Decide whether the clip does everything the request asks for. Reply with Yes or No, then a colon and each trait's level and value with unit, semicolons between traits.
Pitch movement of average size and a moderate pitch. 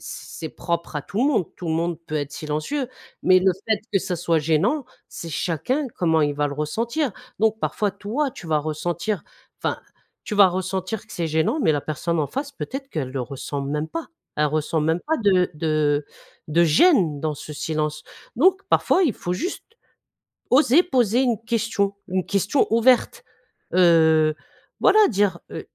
No: wide, 6.7 semitones; medium, 175 Hz